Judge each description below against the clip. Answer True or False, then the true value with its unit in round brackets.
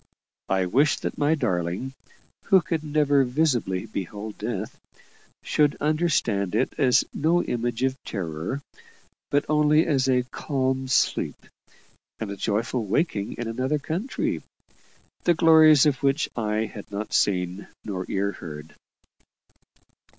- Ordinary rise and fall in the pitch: False (6.5 semitones)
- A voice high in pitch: False (125 Hz)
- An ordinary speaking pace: False (130 wpm)